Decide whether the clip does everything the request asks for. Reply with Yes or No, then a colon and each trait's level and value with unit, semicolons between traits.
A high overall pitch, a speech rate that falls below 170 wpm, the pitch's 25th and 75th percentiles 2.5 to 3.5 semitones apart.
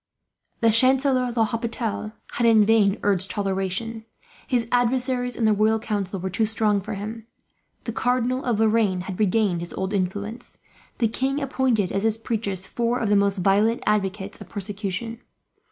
Yes: high, 220 Hz; average, 160 wpm; average, 2.8 semitones